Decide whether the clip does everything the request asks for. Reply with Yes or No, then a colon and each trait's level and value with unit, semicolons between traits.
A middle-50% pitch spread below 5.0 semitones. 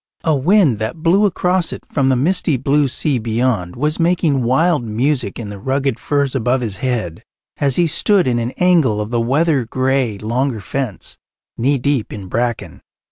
Yes: average, 4.5 semitones